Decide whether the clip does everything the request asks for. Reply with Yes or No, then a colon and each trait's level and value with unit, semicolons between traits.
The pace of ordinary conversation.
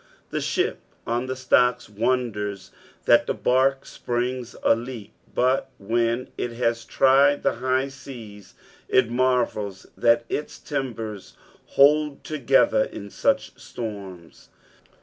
No: slow, 120 wpm